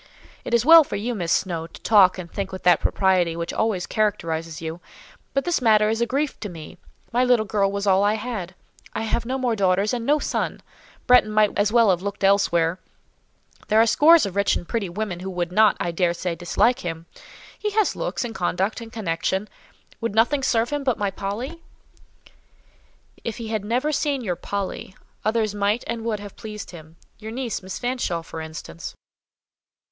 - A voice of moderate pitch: No, high, 210 Hz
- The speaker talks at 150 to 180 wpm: No, average, 195 wpm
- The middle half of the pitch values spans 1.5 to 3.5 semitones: No, average, 4.3 semitones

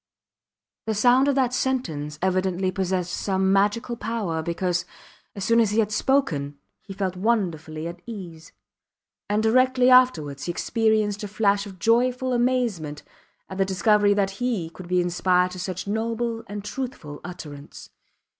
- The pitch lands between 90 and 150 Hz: No, high, 200 Hz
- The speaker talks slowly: No, average, 150 wpm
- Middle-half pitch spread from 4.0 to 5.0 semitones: Yes, average, 4.5 semitones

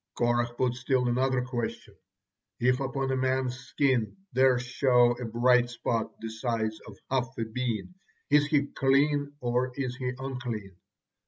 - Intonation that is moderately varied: No, narrow, 1.7 semitones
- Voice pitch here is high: No, low, 125 Hz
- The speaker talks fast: No, average, 150 wpm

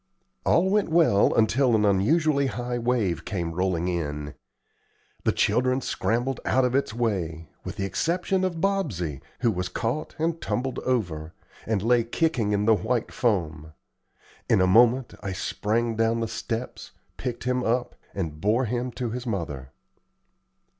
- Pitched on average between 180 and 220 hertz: No, low, 115 Hz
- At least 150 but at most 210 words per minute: Yes, average, 155 wpm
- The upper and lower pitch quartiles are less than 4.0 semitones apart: No, average, 5.2 semitones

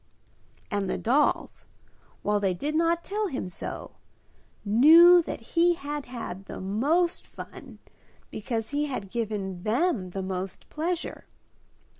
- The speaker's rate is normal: No, slow, 130 wpm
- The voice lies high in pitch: Yes, high, 245 Hz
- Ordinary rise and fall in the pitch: No, wide, 8.7 semitones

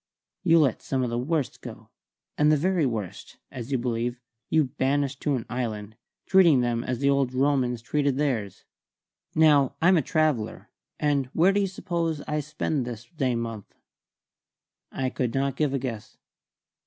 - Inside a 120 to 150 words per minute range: No, average, 165 wpm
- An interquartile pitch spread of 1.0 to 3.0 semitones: No, average, 3.8 semitones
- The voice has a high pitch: No, low, 135 Hz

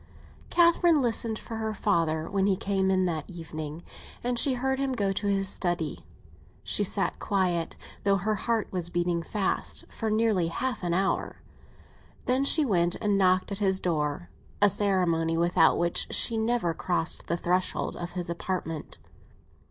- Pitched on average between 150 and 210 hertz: Yes, high, 190 Hz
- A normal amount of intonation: Yes, average, 4.1 semitones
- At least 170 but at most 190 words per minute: No, average, 160 wpm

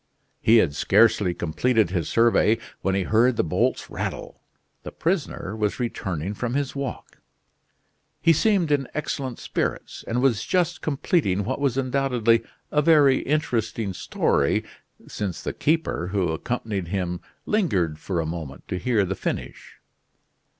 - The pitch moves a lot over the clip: Yes, wide, 6.4 semitones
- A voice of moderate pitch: No, low, 115 Hz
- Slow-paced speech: No, average, 145 wpm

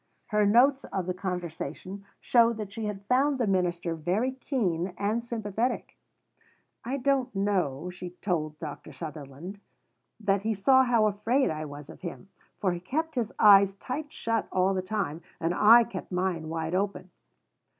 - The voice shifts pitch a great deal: No, average, 4.7 semitones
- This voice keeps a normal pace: Yes, average, 160 wpm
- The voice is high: Yes, high, 195 Hz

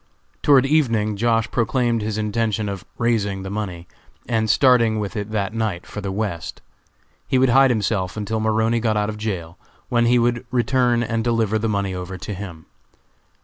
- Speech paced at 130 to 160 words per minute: No, average, 180 wpm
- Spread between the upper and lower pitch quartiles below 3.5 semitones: Yes, narrow, 2.6 semitones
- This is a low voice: Yes, low, 110 Hz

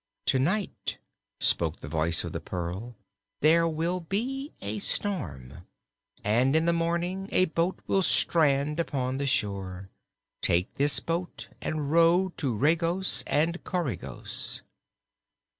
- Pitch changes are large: Yes, wide, 8.2 semitones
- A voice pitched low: No, medium, 155 Hz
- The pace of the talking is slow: Yes, slow, 125 wpm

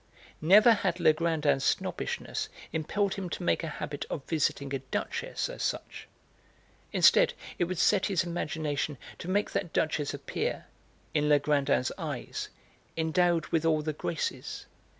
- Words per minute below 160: Yes, average, 140 wpm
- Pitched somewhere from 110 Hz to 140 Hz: No, medium, 160 Hz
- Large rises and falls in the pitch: No, average, 2.9 semitones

